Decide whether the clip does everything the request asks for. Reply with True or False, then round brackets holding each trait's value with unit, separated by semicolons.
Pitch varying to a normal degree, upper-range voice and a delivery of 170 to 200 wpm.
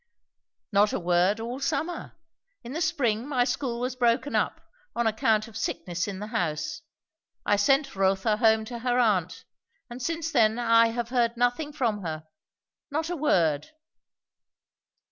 False (3.9 semitones; 230 Hz; 155 wpm)